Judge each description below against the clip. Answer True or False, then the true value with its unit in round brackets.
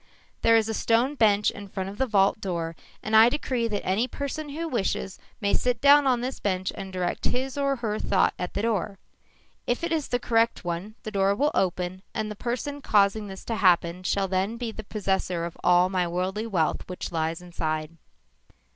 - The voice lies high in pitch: True (205 Hz)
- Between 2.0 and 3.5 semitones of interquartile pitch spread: False (4.3 semitones)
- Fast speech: True (210 wpm)